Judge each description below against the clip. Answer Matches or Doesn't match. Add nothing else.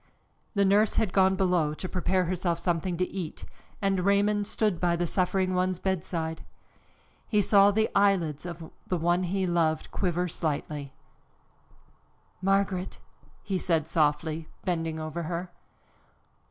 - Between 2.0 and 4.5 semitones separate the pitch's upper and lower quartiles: Matches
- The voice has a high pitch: Doesn't match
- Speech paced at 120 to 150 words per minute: Matches